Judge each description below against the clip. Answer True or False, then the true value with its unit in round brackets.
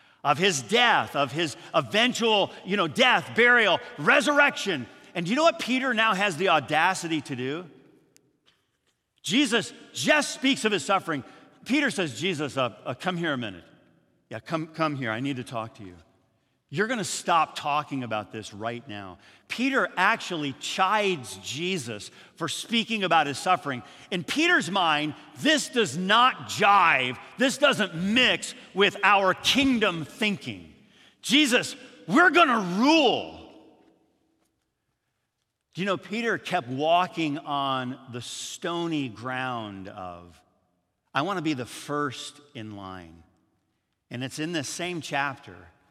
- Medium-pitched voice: True (160 Hz)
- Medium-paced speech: True (145 wpm)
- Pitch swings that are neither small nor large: False (8.9 semitones)